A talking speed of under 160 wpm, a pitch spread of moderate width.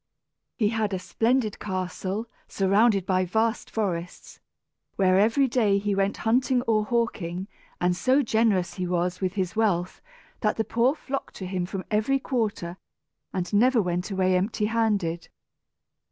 Yes: average, 150 wpm; average, 3.6 semitones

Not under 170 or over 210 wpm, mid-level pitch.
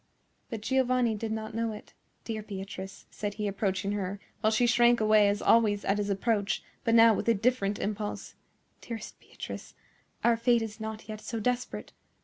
No: average, 175 wpm; high, 220 Hz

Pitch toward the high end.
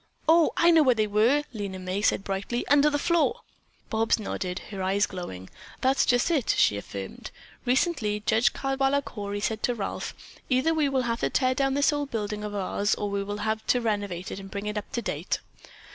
Yes: high, 220 Hz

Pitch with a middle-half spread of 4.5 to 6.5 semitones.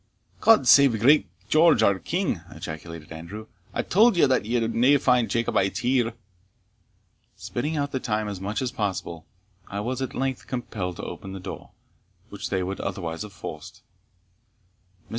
Yes: wide, 5.4 semitones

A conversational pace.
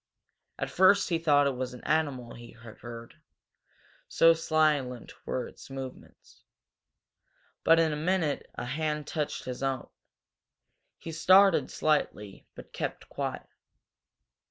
No: slow, 130 wpm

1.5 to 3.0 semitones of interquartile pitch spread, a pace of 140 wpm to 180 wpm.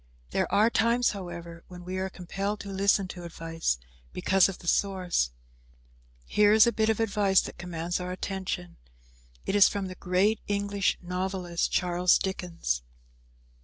Yes: narrow, 2.4 semitones; average, 155 wpm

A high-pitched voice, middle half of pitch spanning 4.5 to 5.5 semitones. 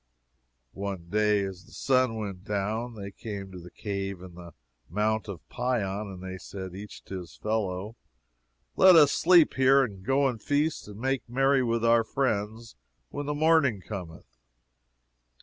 No: low, 105 Hz; average, 4.9 semitones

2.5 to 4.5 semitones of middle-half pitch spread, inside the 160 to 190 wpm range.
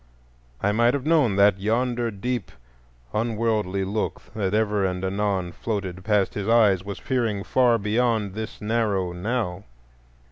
No: average, 3.1 semitones; average, 140 wpm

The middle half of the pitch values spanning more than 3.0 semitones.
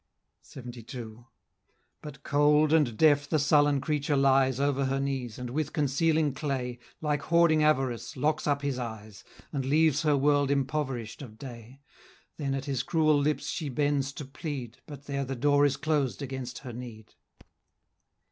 No: narrow, 2.6 semitones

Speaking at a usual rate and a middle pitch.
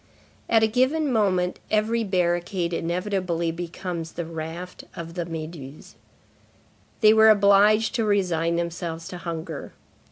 No: slow, 125 wpm; medium, 180 Hz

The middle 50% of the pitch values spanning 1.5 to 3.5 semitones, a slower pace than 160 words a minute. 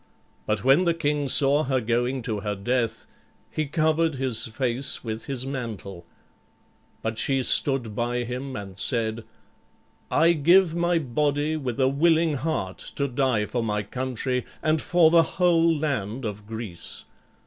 No: average, 5.3 semitones; average, 150 wpm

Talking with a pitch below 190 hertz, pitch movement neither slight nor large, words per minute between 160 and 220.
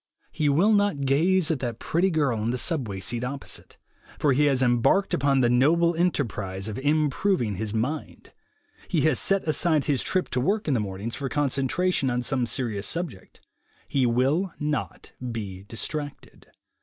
Yes: medium, 140 Hz; average, 5.0 semitones; average, 170 wpm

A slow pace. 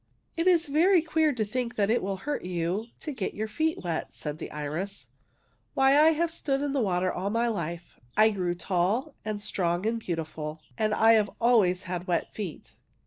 No: average, 200 wpm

